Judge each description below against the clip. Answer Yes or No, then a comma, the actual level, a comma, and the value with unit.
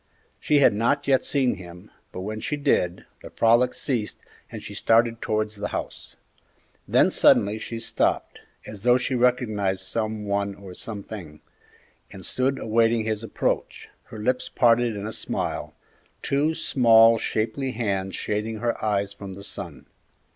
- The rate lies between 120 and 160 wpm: Yes, average, 155 wpm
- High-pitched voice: No, low, 110 Hz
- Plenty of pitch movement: No, average, 3.3 semitones